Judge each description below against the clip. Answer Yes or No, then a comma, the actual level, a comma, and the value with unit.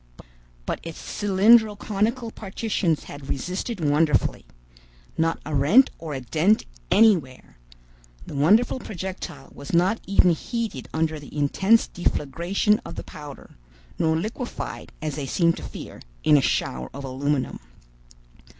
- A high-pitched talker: No, medium, 165 Hz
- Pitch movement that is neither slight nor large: No, wide, 6.2 semitones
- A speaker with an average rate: No, slow, 130 wpm